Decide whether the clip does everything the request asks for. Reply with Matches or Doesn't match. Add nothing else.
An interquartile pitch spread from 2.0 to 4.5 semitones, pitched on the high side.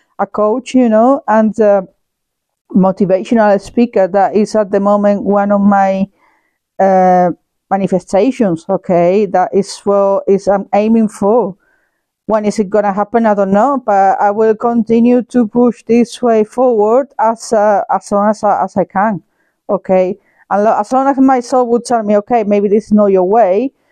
Matches